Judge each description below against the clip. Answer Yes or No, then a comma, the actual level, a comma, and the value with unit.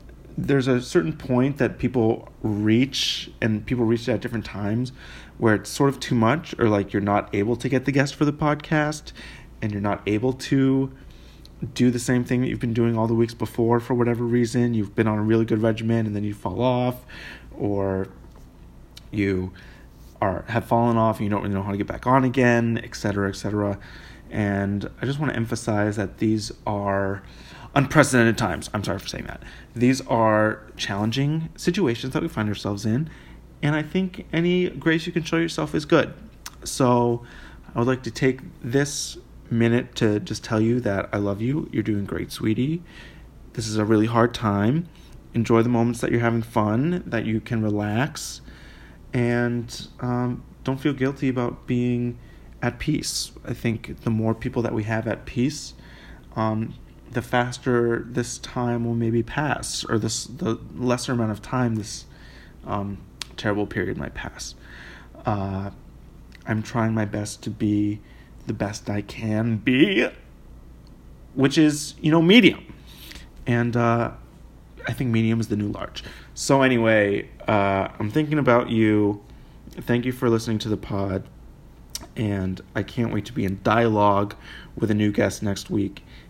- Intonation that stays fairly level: No, average, 3.3 semitones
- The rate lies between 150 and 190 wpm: Yes, average, 175 wpm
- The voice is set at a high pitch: No, low, 115 Hz